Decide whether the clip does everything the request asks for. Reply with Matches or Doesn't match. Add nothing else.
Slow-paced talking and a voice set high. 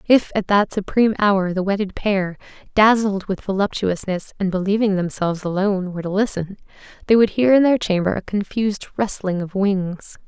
Doesn't match